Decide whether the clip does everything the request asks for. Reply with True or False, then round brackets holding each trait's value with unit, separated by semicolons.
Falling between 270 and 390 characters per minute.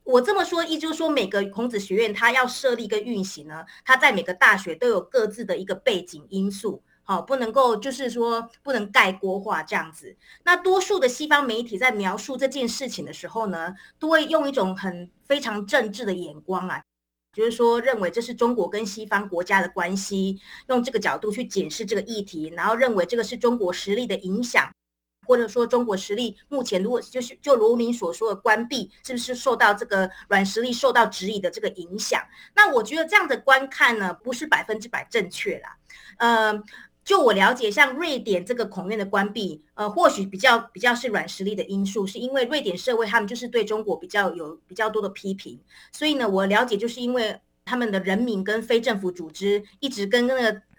True (315 characters per minute)